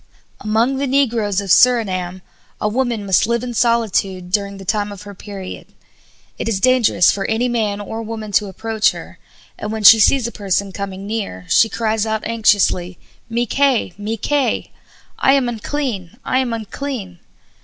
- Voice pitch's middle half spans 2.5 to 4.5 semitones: Yes, average, 3.0 semitones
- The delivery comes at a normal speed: Yes, average, 170 wpm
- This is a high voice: Yes, high, 215 Hz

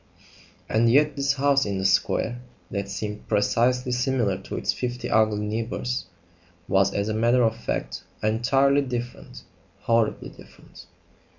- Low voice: Yes, low, 115 Hz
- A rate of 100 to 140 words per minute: Yes, slow, 135 wpm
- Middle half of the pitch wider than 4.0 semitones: No, average, 3.3 semitones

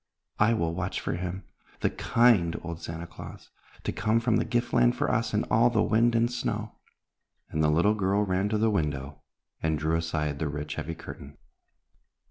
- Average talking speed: Yes, average, 190 wpm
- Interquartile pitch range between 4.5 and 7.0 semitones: Yes, wide, 5.6 semitones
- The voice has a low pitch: Yes, very low, 90 Hz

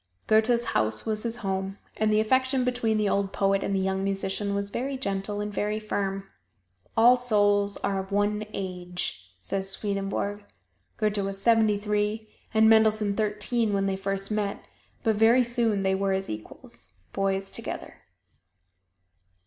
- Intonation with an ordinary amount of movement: No, narrow, 2.0 semitones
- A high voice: Yes, high, 205 Hz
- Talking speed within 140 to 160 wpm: Yes, average, 155 wpm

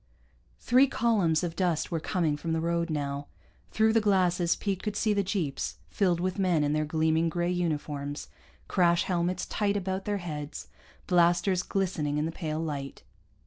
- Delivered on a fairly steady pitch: No, average, 3.3 semitones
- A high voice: No, medium, 175 Hz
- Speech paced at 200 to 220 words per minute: No, average, 170 wpm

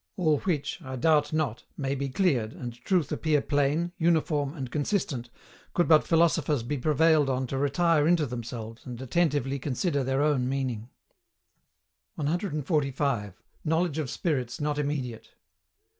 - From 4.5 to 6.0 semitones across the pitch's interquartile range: No, average, 3.6 semitones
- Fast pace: No, average, 140 wpm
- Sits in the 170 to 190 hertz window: No, medium, 145 Hz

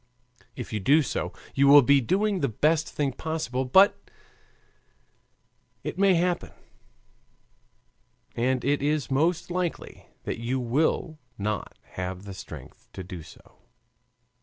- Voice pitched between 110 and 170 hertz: Yes, medium, 140 Hz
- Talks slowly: Yes, slow, 130 wpm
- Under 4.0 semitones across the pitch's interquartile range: No, wide, 5.5 semitones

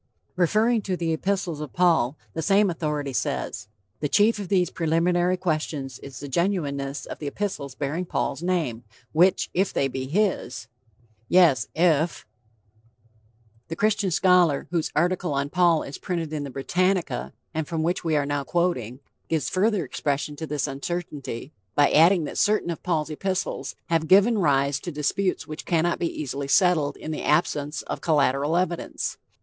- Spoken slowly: No, average, 165 wpm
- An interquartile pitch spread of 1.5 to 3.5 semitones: No, average, 4.0 semitones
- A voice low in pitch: No, medium, 160 Hz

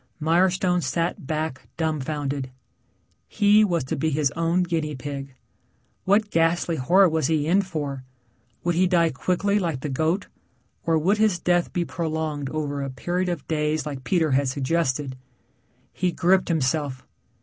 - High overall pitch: No, medium, 160 Hz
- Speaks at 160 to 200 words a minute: No, average, 150 wpm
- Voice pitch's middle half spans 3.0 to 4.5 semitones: Yes, average, 3.6 semitones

